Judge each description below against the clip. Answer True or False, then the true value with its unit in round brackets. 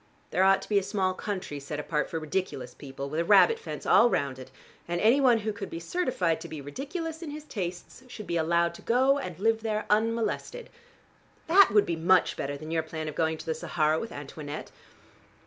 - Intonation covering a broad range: True (6.3 semitones)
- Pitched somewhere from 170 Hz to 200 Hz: True (185 Hz)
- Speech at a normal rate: False (215 wpm)